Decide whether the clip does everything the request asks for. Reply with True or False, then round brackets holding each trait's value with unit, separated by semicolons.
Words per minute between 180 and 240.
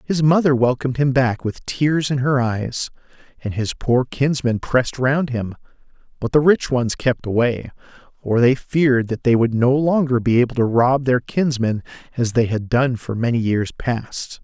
True (185 wpm)